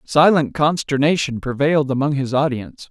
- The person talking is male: Yes, male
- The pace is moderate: No, slow, 125 wpm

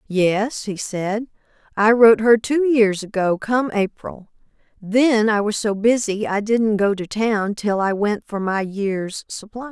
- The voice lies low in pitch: No, high, 210 Hz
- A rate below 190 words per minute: Yes, average, 175 wpm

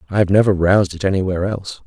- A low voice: Yes, very low, 95 Hz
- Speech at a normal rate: No, fast, 225 wpm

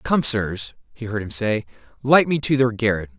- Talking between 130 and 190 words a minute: No, fast, 205 wpm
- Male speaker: Yes, male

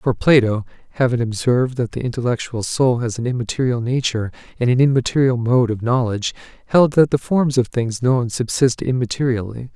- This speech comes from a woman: No, male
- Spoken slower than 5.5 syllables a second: No, 5.6 syllables/s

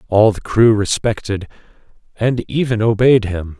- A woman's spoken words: No, male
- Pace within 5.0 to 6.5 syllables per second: No, 4.4 syllables/s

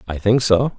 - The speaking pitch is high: No, low, 110 Hz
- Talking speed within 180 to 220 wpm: No, fast, 230 wpm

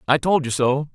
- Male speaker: Yes, male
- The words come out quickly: Yes, fast, 255 wpm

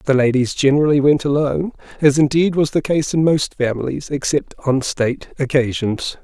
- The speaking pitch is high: No, medium, 140 Hz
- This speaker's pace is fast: No, average, 165 wpm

